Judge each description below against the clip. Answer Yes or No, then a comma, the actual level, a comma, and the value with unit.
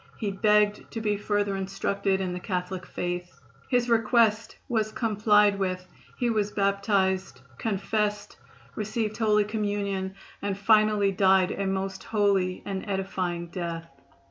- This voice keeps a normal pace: No, slow, 130 wpm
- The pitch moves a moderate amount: No, narrow, 1.8 semitones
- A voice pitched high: Yes, high, 200 Hz